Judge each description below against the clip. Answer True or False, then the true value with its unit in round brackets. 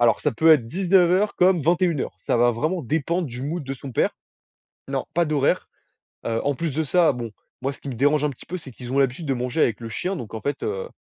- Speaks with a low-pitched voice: False (145 Hz)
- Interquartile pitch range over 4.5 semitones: True (5.6 semitones)